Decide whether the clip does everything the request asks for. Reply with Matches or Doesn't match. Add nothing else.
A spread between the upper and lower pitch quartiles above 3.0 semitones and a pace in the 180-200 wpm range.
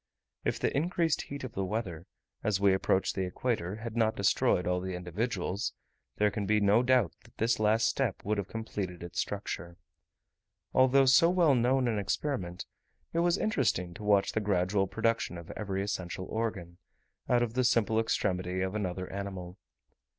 Doesn't match